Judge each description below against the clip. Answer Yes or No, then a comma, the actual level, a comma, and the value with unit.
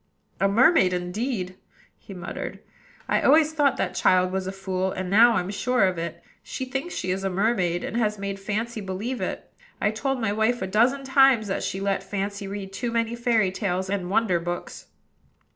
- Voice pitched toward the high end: Yes, high, 200 Hz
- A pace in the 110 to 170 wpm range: No, average, 195 wpm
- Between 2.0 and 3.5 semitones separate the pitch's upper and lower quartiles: No, average, 4.1 semitones